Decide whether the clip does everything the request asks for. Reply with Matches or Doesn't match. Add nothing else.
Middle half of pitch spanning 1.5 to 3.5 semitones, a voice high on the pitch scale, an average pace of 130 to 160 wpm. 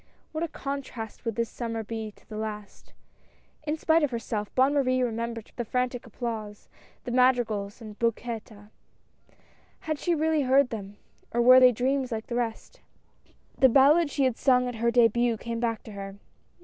Doesn't match